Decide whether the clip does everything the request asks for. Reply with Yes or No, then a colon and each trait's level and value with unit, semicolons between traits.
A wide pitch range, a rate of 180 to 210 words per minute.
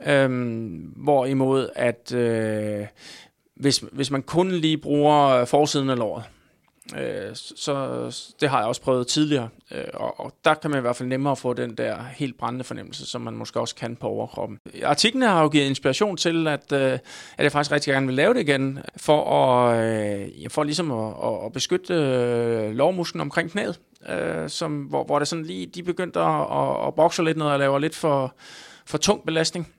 No: average, 4.0 semitones; average, 190 wpm